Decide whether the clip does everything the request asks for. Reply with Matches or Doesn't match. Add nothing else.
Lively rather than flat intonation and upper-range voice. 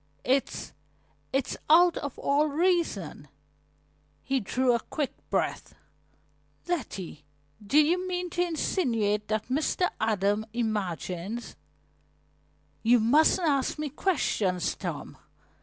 Matches